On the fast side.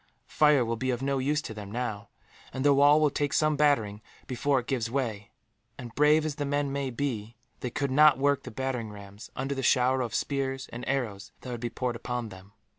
Yes: fast, 220 wpm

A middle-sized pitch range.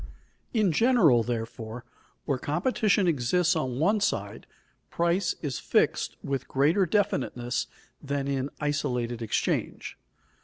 No: wide, 6.4 semitones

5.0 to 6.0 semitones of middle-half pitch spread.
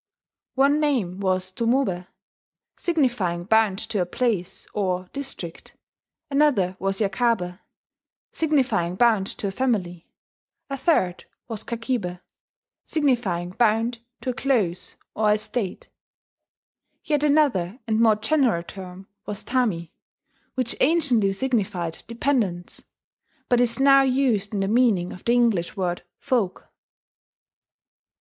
Yes: wide, 5.6 semitones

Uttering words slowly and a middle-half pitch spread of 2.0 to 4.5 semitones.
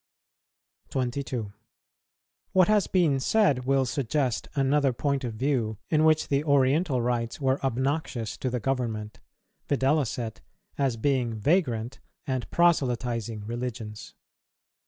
Yes: slow, 115 wpm; average, 3.3 semitones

